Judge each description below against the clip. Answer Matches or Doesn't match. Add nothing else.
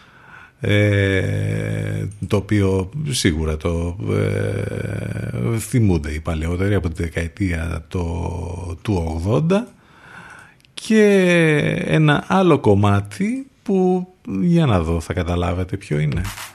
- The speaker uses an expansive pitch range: Matches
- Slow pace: Matches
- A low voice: Matches